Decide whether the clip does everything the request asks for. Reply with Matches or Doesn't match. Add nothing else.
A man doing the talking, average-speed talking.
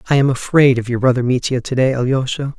Doesn't match